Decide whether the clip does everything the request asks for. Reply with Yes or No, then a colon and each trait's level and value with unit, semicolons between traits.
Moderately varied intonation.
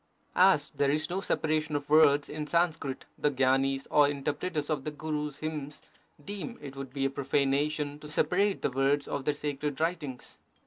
No: narrow, 1.9 semitones